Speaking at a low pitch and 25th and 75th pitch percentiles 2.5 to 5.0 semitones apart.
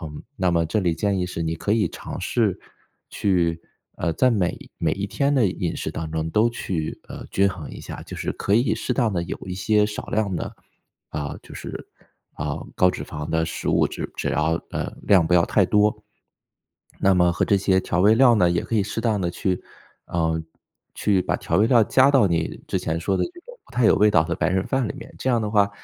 Yes: very low, 95 Hz; average, 4.2 semitones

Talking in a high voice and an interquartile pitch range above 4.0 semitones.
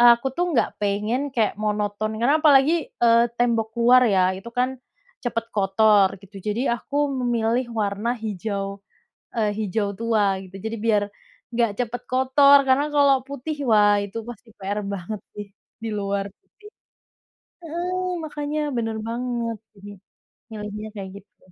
No: high, 225 Hz; average, 3.4 semitones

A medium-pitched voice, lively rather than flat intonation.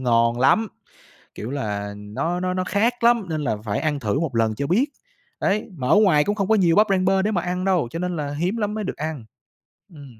Yes: medium, 165 Hz; wide, 7.4 semitones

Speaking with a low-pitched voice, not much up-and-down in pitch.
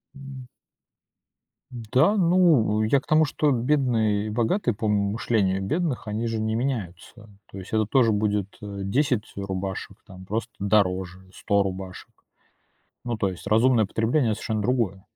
No: low, 110 Hz; average, 3.9 semitones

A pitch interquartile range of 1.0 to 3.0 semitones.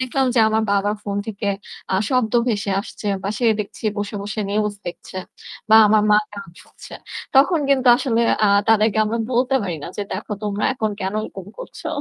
Yes: narrow, 2.5 semitones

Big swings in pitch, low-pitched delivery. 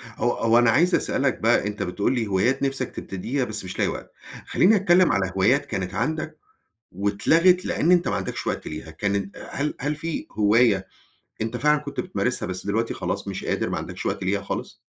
Yes: wide, 6.7 semitones; low, 115 Hz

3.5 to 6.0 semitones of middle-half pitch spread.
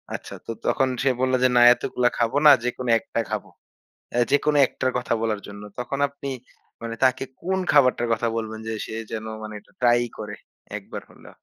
No: narrow, 2.6 semitones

